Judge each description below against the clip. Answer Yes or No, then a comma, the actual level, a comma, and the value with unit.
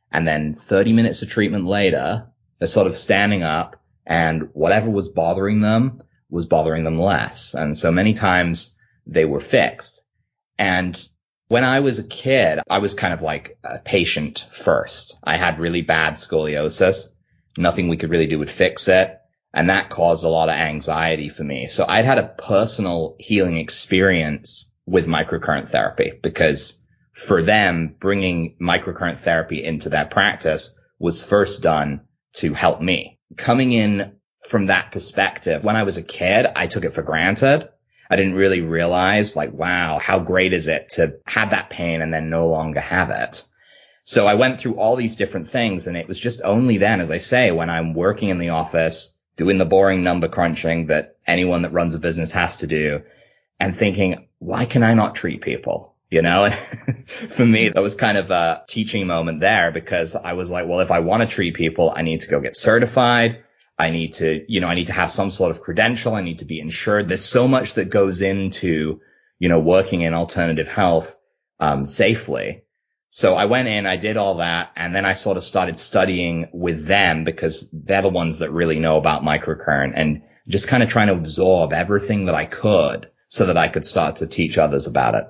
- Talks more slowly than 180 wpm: No, average, 195 wpm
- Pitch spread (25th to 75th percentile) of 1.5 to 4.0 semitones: Yes, average, 3.6 semitones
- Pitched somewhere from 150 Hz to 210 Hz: No, very low, 90 Hz